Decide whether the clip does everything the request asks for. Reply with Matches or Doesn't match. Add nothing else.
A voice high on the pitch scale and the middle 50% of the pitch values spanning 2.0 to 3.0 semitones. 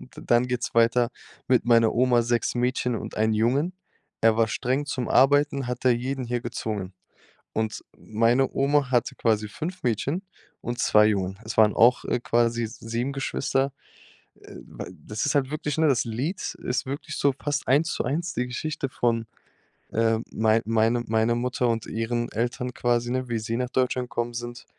Doesn't match